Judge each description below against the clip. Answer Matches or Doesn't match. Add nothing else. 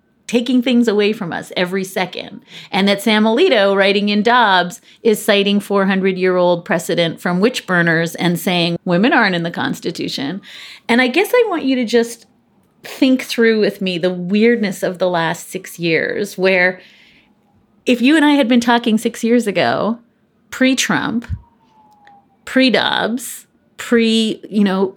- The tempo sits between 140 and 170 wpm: Matches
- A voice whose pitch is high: Matches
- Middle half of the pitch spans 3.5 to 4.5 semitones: Matches